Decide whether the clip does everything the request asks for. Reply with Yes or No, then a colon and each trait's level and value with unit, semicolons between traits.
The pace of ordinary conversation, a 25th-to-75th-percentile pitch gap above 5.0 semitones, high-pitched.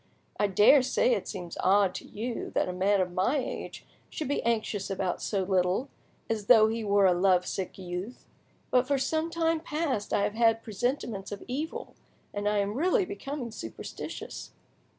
Yes: average, 175 wpm; wide, 5.5 semitones; high, 215 Hz